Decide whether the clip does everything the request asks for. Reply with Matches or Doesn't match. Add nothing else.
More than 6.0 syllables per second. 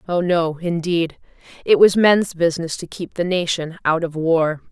Doesn't match